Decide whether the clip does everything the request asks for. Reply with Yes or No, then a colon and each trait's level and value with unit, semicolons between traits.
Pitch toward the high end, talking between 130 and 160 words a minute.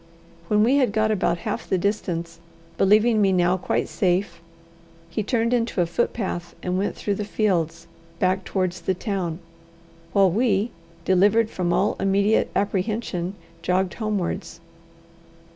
Yes: high, 195 Hz; average, 140 wpm